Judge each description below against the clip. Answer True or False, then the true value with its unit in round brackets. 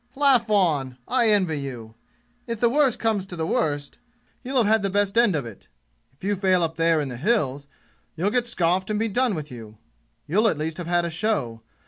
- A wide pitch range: True (6.8 semitones)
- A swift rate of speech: True (215 wpm)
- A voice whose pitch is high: False (180 Hz)